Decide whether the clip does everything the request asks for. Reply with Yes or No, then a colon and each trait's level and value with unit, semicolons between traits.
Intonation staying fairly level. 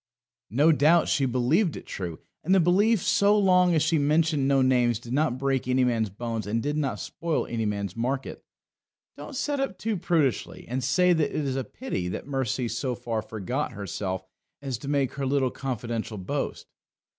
No: wide, 5.5 semitones